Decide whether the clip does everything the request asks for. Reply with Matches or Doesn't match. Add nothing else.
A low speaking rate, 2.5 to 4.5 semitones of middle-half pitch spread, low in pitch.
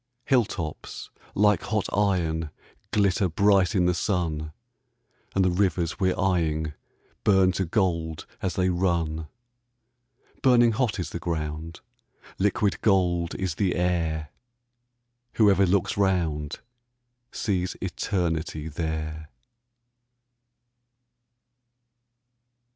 Matches